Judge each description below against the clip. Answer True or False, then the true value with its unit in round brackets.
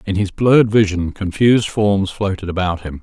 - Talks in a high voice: False (95 Hz)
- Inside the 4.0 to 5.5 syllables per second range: True (5.2 syllables/s)